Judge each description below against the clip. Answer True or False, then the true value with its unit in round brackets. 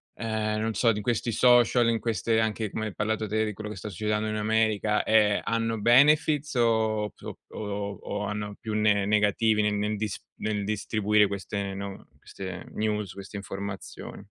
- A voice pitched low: True (105 Hz)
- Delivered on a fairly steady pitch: True (1.4 semitones)